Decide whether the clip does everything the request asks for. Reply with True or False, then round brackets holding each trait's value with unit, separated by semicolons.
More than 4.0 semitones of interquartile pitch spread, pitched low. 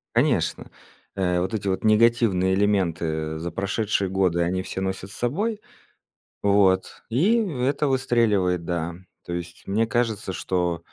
True (4.5 semitones; 95 Hz)